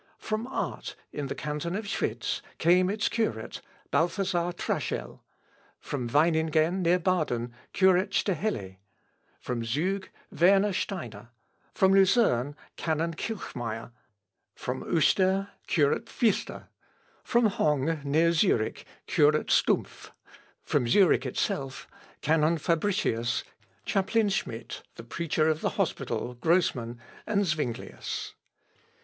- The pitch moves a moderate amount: No, wide, 5.9 semitones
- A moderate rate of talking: No, slow, 105 wpm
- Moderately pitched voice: Yes, medium, 165 Hz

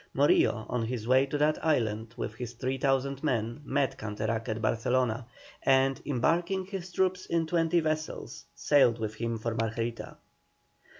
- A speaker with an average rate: Yes, average, 145 wpm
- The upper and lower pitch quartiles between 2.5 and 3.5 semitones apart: No, average, 4.9 semitones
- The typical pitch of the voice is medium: No, low, 130 Hz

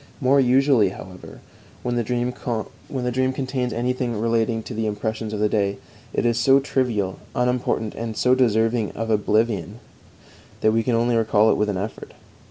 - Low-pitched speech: Yes, low, 115 Hz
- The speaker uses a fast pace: No, average, 165 wpm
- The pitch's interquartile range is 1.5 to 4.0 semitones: Yes, narrow, 2.5 semitones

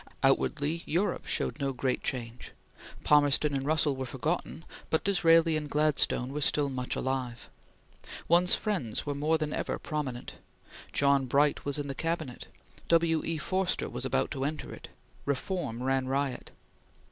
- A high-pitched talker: No, medium, 145 Hz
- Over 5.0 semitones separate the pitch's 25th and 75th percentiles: No, average, 3.2 semitones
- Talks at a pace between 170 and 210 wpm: No, average, 150 wpm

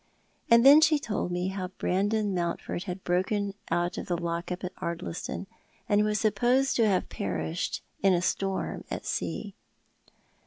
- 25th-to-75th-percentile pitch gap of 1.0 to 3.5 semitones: Yes, average, 3.2 semitones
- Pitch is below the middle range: No, high, 190 Hz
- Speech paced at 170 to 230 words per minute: No, average, 160 wpm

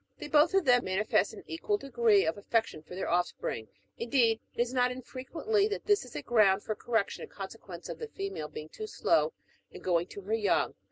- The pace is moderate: No, fast, 215 wpm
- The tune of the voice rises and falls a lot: Yes, wide, 7.6 semitones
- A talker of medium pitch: No, high, 235 Hz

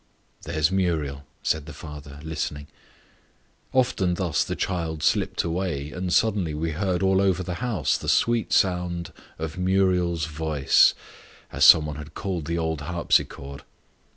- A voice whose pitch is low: Yes, very low, 85 Hz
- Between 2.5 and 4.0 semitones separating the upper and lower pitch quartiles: Yes, average, 3.5 semitones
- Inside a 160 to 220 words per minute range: No, average, 145 wpm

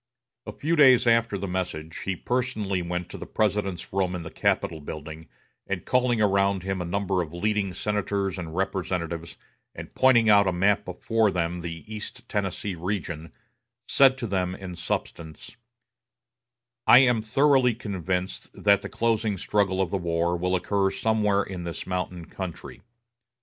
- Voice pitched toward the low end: Yes, very low, 95 Hz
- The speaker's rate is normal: Yes, average, 160 wpm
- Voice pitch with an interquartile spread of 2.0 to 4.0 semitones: Yes, average, 3.2 semitones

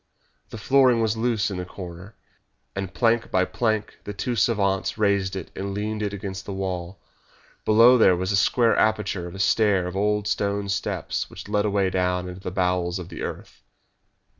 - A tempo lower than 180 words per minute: No, average, 190 wpm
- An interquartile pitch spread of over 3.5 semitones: No, narrow, 2.6 semitones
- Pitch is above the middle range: No, low, 100 Hz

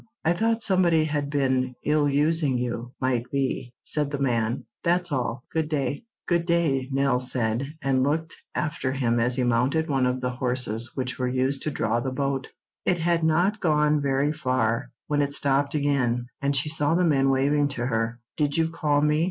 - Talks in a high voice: No, medium, 140 Hz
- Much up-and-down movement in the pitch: No, average, 3.2 semitones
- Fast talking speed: No, average, 190 wpm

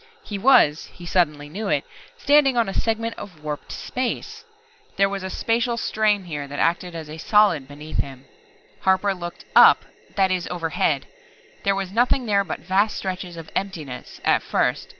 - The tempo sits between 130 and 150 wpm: No, average, 170 wpm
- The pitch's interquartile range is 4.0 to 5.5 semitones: Yes, average, 5.0 semitones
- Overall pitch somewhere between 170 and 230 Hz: Yes, high, 190 Hz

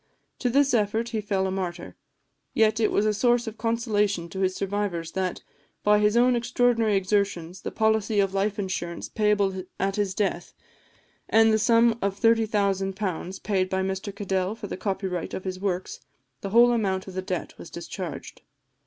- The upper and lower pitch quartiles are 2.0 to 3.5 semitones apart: Yes, narrow, 2.5 semitones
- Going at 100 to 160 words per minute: No, average, 175 wpm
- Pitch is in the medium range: No, high, 200 Hz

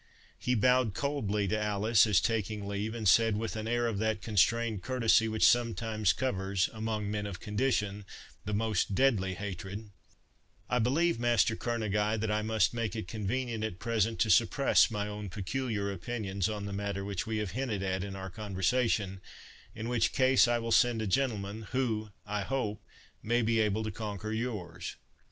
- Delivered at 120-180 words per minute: Yes, average, 175 wpm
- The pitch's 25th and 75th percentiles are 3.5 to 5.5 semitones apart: No, narrow, 2.5 semitones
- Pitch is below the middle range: Yes, low, 110 Hz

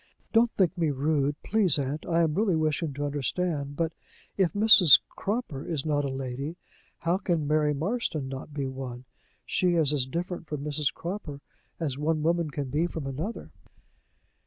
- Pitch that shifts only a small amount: No, average, 3.5 semitones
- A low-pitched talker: No, medium, 155 Hz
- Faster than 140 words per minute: Yes, average, 170 wpm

